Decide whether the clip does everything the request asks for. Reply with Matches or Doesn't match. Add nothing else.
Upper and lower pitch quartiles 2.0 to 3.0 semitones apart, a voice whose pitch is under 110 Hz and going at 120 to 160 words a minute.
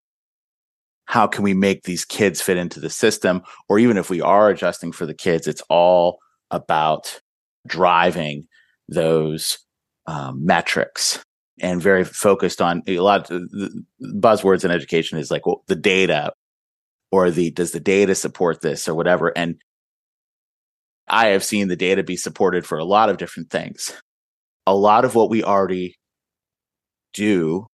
Matches